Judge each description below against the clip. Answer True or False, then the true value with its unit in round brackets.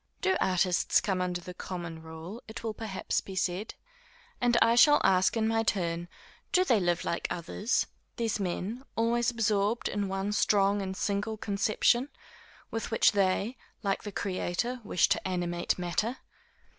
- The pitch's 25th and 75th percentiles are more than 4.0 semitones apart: False (3.7 semitones)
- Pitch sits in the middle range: False (200 Hz)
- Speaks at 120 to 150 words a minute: False (160 wpm)